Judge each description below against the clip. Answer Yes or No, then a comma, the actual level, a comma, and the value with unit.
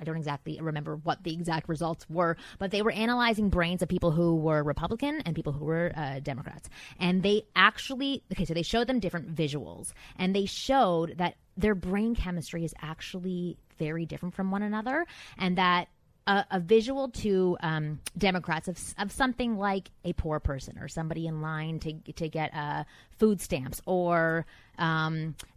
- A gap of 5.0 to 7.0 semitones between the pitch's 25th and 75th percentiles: No, average, 3.8 semitones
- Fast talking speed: No, average, 180 wpm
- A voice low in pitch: No, medium, 170 Hz